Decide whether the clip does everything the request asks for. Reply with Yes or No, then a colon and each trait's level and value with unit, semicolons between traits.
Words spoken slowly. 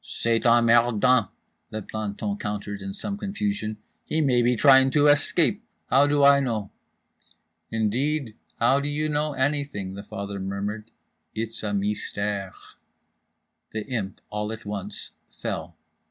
Yes: slow, 130 wpm